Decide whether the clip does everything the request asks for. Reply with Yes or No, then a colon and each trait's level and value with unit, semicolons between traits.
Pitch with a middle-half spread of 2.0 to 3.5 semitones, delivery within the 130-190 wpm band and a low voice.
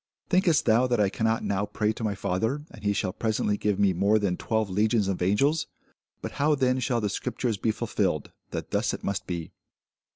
No: average, 3.2 semitones; fast, 205 wpm; low, 105 Hz